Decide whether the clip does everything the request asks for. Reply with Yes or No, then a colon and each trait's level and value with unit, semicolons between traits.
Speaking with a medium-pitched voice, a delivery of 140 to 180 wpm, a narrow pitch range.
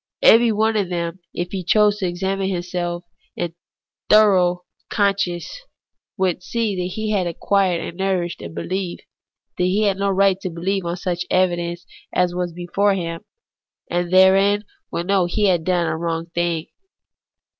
Yes: medium, 180 Hz; average, 165 wpm; narrow, 2.2 semitones